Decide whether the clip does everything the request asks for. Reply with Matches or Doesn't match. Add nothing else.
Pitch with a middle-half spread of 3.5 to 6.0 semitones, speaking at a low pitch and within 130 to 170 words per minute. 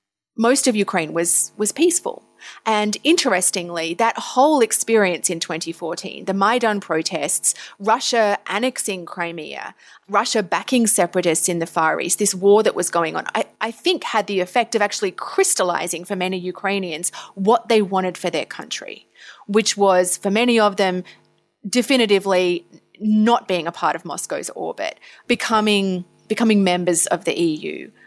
Doesn't match